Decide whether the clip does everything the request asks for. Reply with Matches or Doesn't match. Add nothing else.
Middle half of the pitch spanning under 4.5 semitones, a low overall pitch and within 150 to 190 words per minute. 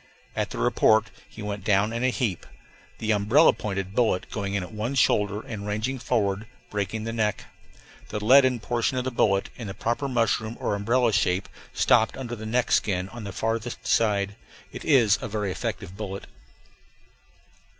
Matches